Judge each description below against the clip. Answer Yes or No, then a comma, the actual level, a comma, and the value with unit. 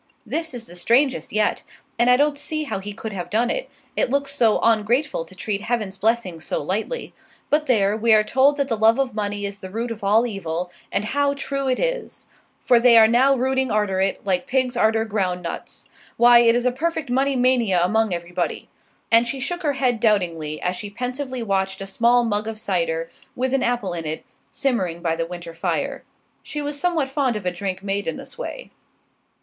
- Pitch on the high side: Yes, high, 225 Hz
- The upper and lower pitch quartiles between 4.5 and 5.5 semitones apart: Yes, average, 5.1 semitones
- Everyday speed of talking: No, fast, 210 wpm